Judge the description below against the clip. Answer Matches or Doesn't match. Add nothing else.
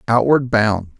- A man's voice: Matches